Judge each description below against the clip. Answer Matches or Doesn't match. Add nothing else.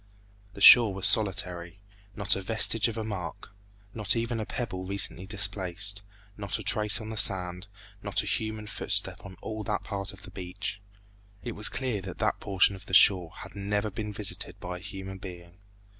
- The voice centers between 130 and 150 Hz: Doesn't match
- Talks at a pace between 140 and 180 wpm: Doesn't match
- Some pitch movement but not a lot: Doesn't match